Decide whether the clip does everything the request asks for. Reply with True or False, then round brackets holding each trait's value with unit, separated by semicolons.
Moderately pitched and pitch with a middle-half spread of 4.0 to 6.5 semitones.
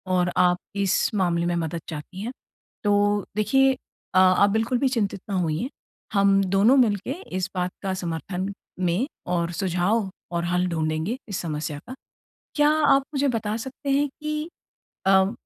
False (195 Hz; 4.3 semitones)